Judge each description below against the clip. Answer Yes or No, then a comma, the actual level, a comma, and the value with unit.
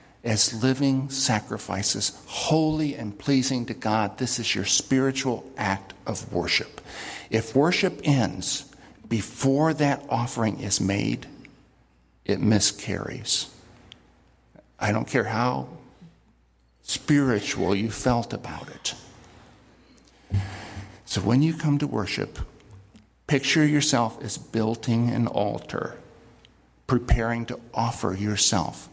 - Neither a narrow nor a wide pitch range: Yes, average, 4.9 semitones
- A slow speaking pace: Yes, slow, 105 wpm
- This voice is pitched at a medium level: No, low, 115 Hz